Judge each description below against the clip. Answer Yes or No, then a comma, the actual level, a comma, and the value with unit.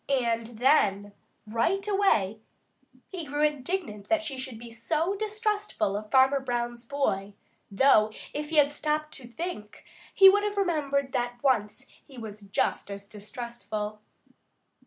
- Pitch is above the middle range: Yes, very high, 260 Hz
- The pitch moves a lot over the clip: Yes, wide, 6.2 semitones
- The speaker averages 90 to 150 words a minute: Yes, average, 140 wpm